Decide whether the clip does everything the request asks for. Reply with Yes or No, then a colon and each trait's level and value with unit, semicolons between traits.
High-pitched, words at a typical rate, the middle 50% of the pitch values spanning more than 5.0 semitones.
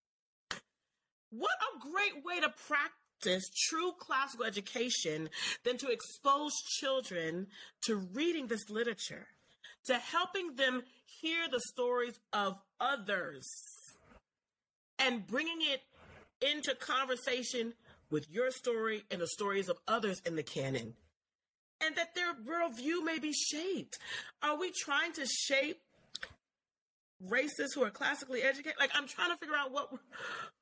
No: very high, 260 Hz; slow, 125 wpm; wide, 5.5 semitones